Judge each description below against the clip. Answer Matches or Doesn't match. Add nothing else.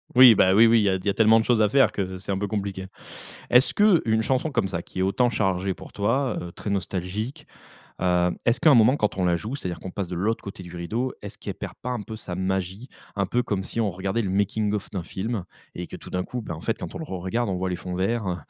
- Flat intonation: Doesn't match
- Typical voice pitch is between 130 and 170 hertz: Doesn't match